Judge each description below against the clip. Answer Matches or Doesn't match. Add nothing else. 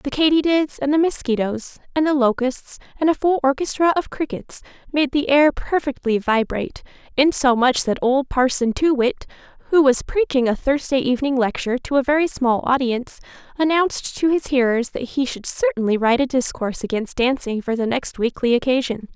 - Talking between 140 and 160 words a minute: Doesn't match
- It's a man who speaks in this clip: Doesn't match